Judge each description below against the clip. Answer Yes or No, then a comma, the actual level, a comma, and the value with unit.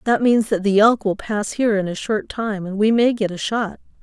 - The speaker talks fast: Yes, fast, 270 wpm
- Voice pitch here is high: Yes, high, 210 Hz